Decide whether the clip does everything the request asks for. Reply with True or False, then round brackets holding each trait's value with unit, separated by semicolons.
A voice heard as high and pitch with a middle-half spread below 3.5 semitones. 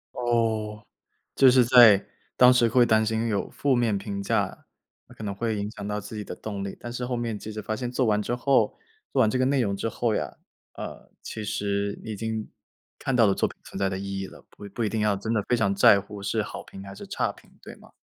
False (110 Hz; 2.9 semitones)